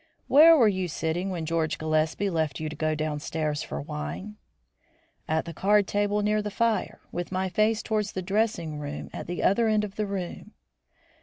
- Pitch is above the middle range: No, medium, 180 Hz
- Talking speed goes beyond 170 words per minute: Yes, average, 185 wpm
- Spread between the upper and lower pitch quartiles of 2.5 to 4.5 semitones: No, average, 5.0 semitones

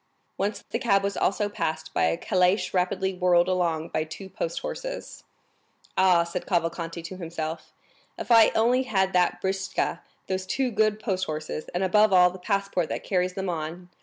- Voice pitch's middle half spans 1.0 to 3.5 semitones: Yes, average, 2.7 semitones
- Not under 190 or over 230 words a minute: No, average, 175 wpm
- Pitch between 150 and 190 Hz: Yes, medium, 185 Hz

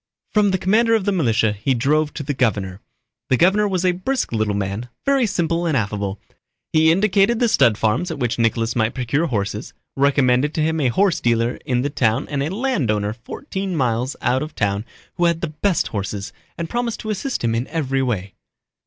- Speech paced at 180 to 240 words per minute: Yes, average, 200 wpm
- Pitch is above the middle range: No, medium, 140 Hz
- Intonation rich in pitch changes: Yes, wide, 8.0 semitones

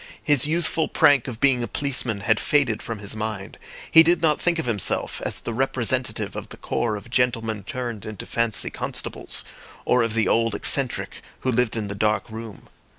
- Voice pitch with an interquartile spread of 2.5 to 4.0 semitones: Yes, average, 3.5 semitones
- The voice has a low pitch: Yes, low, 115 Hz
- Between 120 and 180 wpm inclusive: No, average, 190 wpm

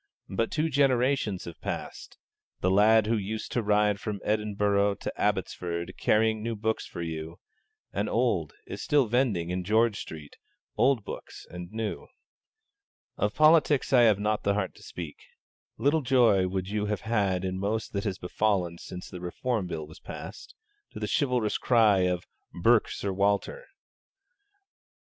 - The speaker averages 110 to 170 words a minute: Yes, average, 160 wpm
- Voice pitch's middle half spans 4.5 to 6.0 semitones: No, average, 3.7 semitones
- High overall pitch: No, low, 105 Hz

